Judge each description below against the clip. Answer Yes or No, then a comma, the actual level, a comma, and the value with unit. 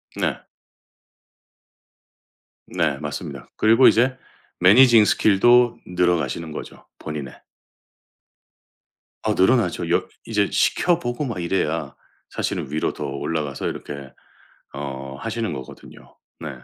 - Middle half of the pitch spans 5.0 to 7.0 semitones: No, wide, 7.4 semitones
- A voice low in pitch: Yes, very low, 90 Hz